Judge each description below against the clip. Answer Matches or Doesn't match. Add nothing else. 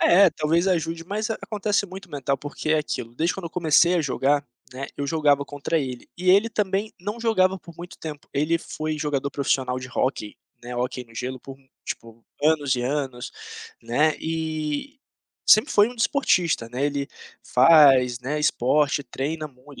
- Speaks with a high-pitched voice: Doesn't match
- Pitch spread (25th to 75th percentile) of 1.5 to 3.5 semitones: Doesn't match